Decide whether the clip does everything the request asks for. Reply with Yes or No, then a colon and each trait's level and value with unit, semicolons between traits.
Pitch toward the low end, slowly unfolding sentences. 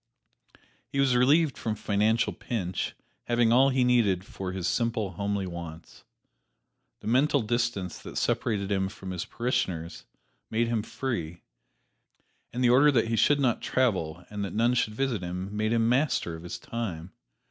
No: low, 110 Hz; average, 160 wpm